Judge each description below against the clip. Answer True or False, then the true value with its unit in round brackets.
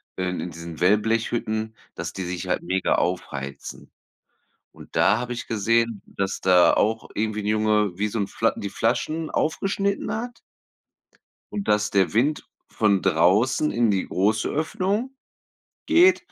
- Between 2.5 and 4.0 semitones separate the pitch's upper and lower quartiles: False (4.4 semitones)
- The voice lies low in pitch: True (110 Hz)